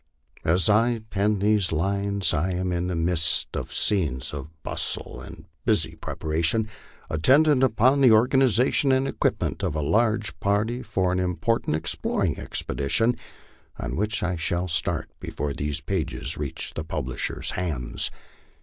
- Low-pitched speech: Yes, very low, 95 Hz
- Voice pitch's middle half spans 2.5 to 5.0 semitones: No, wide, 5.5 semitones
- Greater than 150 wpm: No, average, 145 wpm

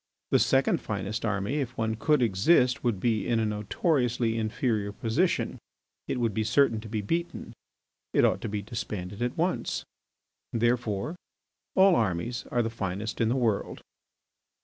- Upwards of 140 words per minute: Yes, average, 155 wpm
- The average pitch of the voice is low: Yes, low, 115 Hz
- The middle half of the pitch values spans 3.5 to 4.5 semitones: No, average, 2.9 semitones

